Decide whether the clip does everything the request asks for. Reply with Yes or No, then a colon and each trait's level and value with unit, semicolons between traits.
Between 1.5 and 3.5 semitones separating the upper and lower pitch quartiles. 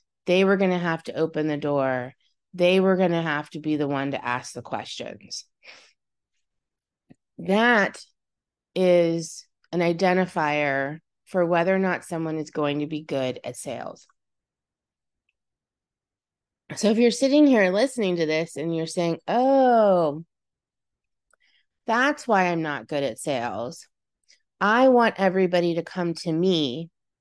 No: average, 3.9 semitones